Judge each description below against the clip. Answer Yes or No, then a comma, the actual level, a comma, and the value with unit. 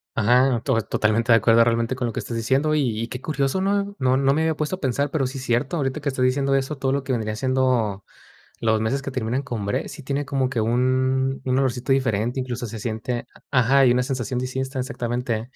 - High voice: No, low, 130 Hz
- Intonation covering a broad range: No, average, 2.7 semitones